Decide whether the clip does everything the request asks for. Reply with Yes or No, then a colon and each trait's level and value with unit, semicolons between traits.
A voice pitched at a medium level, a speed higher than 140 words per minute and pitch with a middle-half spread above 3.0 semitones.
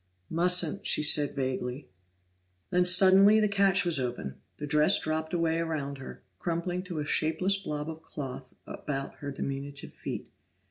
Yes: medium, 160 Hz; average, 150 wpm; average, 4.2 semitones